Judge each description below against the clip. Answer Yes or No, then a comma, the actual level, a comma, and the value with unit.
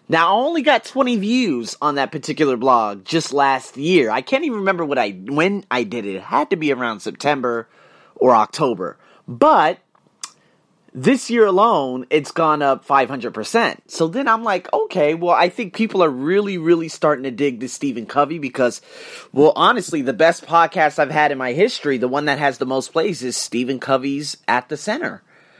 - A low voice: No, medium, 150 Hz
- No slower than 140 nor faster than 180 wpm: No, average, 190 wpm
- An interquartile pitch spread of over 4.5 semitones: Yes, wide, 5.6 semitones